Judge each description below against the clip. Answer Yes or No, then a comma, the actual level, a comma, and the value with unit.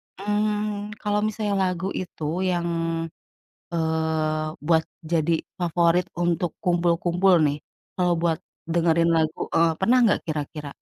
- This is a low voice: No, medium, 170 Hz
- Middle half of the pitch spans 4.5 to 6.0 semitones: No, average, 2.8 semitones